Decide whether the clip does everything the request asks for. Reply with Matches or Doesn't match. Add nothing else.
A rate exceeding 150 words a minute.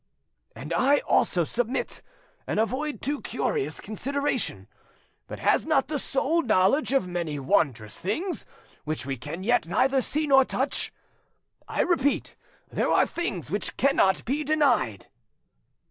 Doesn't match